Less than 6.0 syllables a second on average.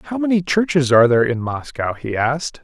Yes: 5.8 syllables/s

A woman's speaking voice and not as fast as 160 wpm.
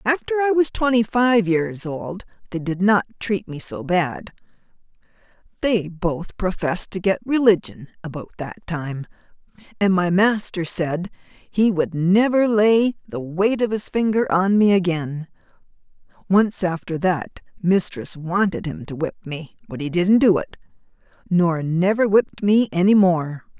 Yes: female; average, 150 wpm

